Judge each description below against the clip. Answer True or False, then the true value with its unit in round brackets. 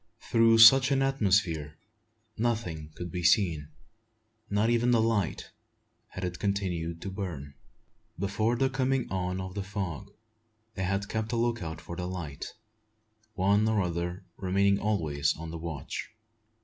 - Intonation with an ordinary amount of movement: True (4.5 semitones)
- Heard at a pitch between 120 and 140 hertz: False (95 Hz)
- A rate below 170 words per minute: True (150 wpm)